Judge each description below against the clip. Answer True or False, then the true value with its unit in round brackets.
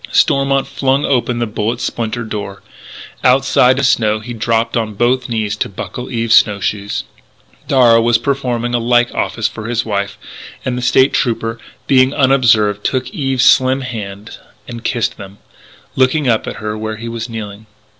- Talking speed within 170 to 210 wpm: True (175 wpm)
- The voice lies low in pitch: True (120 Hz)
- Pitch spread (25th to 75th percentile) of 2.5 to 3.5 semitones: True (2.9 semitones)